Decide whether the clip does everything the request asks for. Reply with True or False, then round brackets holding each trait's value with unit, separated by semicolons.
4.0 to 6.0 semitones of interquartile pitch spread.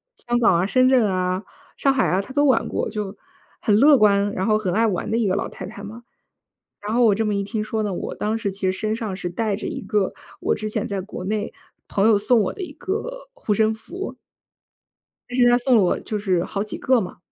False (3.2 semitones)